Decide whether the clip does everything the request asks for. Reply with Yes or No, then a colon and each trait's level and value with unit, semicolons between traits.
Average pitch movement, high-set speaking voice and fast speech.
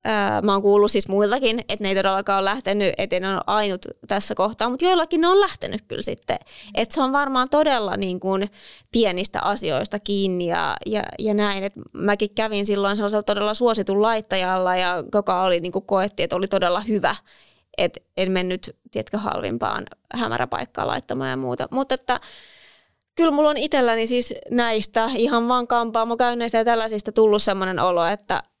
Yes: average, 3.4 semitones; high, 210 Hz; fast, 175 wpm